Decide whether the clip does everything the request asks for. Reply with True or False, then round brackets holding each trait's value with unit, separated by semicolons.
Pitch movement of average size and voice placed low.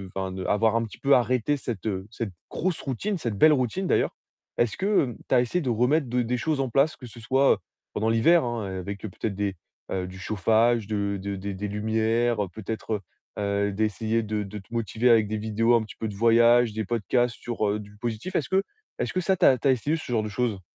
True (3.1 semitones; 115 Hz)